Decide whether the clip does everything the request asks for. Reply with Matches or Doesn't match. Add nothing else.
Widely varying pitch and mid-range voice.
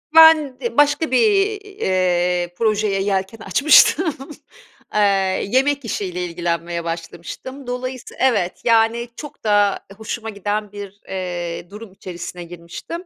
Doesn't match